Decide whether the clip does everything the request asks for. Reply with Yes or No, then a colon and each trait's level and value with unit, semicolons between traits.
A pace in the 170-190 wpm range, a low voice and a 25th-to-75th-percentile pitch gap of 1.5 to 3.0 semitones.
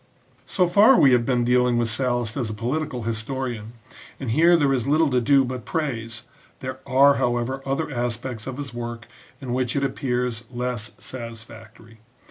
Yes: average, 175 wpm; low, 125 Hz; average, 2.7 semitones